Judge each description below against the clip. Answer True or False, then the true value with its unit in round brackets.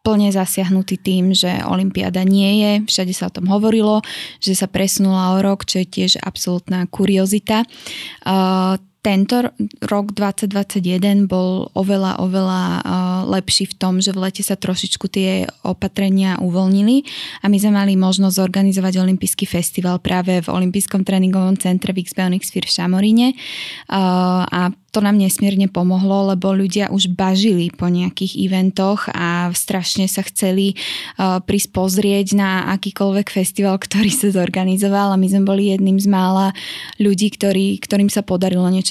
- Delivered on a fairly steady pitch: True (1.2 semitones)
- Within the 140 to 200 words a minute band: True (145 wpm)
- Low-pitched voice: False (190 Hz)